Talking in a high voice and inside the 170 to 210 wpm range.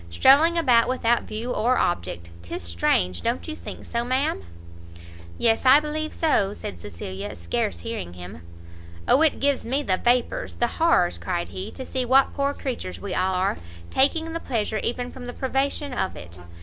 Yes: high, 240 Hz; average, 175 wpm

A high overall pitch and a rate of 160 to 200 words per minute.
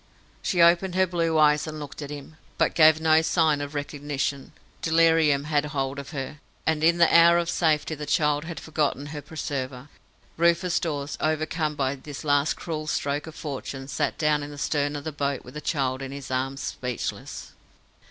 No: medium, 150 Hz; average, 190 wpm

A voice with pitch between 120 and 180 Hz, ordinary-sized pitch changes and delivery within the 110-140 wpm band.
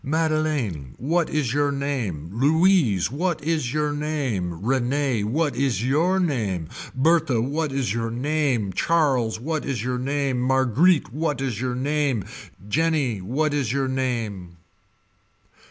Yes: low, 135 Hz; average, 4.6 semitones; slow, 135 wpm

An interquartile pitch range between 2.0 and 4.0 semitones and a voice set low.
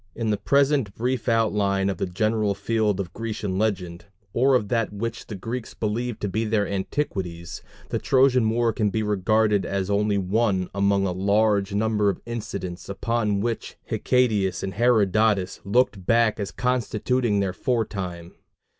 Yes: average, 2.8 semitones; low, 105 Hz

